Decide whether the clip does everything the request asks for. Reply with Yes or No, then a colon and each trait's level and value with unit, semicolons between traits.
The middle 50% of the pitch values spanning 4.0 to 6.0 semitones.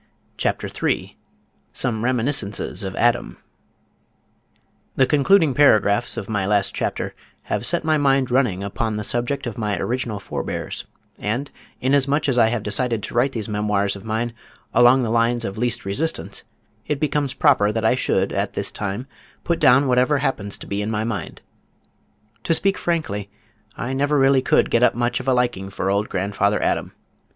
Yes: average, 4.5 semitones